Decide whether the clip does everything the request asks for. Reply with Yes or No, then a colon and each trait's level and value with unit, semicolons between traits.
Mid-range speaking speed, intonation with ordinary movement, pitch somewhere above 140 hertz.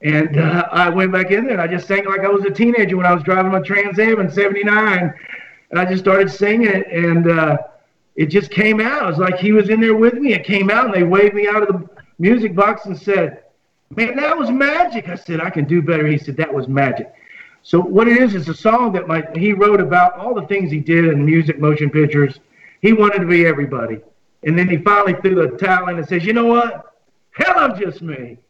No: fast, 250 wpm; average, 3.9 semitones; high, 190 Hz